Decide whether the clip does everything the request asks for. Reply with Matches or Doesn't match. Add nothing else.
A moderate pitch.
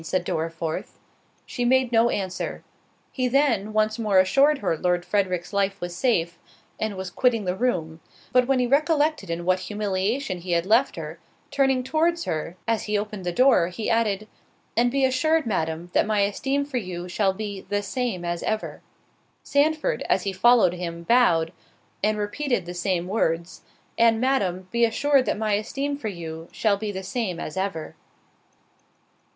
Doesn't match